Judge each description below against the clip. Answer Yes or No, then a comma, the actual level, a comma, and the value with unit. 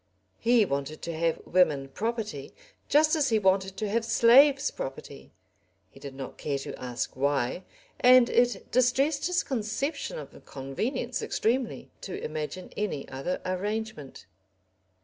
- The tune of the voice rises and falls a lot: Yes, wide, 9.0 semitones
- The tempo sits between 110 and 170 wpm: Yes, slow, 135 wpm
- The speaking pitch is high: Yes, high, 205 Hz